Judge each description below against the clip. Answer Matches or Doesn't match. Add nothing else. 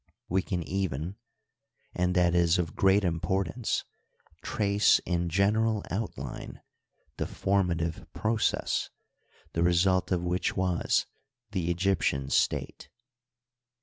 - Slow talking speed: Matches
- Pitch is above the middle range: Doesn't match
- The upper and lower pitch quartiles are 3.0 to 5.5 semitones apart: Doesn't match